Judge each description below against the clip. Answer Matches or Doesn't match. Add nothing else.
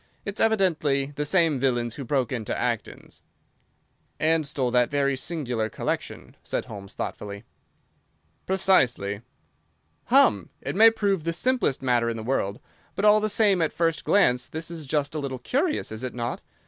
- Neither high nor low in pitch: Matches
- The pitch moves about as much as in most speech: Doesn't match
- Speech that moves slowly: Doesn't match